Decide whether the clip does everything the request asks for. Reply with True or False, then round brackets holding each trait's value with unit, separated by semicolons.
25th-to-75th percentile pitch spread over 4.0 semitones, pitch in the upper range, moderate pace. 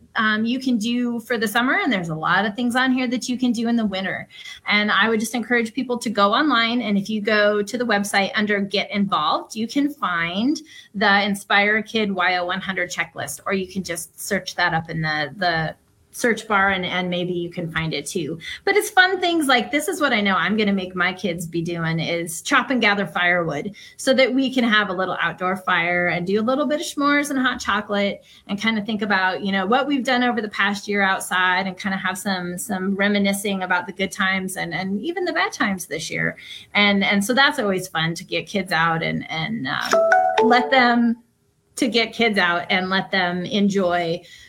False (4.8 semitones; 205 Hz; 225 wpm)